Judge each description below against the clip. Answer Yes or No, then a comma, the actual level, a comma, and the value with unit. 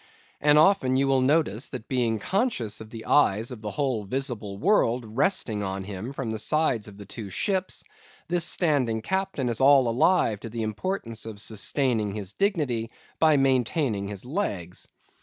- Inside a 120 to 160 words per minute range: No, average, 170 wpm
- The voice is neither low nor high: No, low, 120 Hz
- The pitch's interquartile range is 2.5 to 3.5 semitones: No, wide, 5.4 semitones